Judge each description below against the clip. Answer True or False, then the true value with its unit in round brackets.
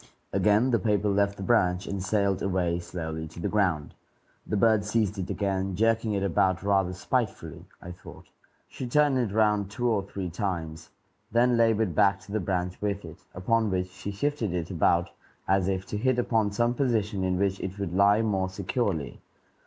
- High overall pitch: False (100 Hz)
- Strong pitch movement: False (2.9 semitones)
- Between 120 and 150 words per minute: False (185 wpm)